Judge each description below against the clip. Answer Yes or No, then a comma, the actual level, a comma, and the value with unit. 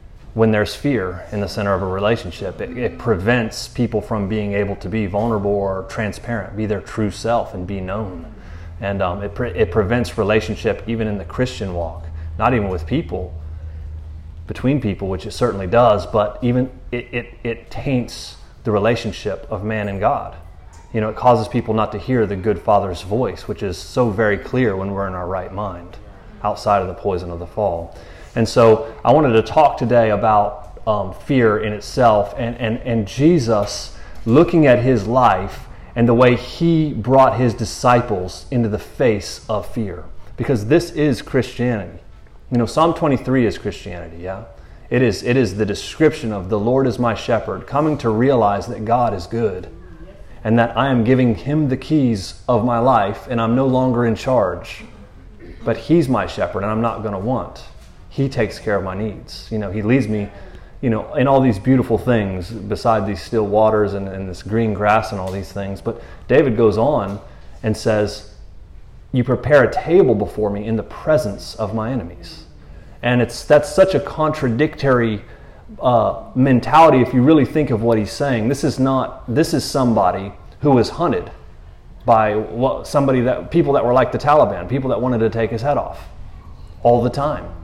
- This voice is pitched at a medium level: No, low, 110 Hz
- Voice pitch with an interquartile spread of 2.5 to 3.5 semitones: No, average, 3.9 semitones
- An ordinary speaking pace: Yes, average, 190 wpm